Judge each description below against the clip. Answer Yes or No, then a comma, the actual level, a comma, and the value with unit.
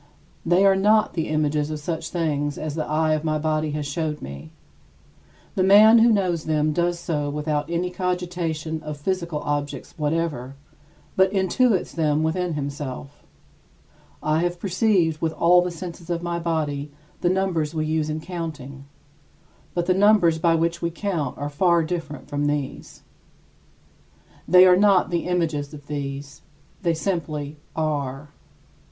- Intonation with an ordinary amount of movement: Yes, average, 3.0 semitones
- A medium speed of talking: Yes, average, 155 wpm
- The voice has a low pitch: No, medium, 160 Hz